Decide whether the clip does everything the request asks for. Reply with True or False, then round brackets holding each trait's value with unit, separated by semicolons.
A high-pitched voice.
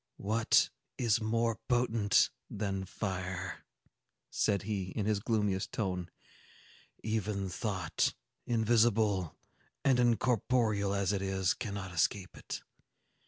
False (105 Hz)